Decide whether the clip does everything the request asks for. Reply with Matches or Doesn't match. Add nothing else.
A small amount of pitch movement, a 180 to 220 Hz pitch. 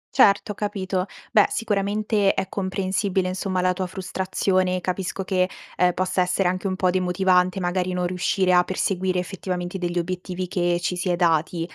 Matches